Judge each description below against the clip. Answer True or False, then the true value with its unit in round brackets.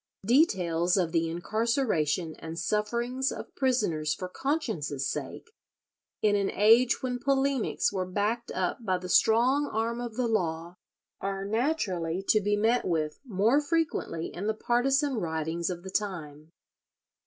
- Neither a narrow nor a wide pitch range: False (5.9 semitones)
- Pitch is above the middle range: True (205 Hz)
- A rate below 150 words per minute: True (140 wpm)